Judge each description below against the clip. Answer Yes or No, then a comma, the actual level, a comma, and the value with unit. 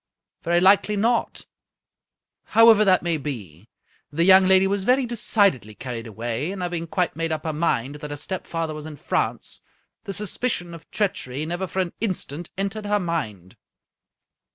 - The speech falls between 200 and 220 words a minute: No, average, 165 wpm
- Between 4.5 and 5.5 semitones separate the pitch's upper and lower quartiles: Yes, average, 5.1 semitones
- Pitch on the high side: No, medium, 175 Hz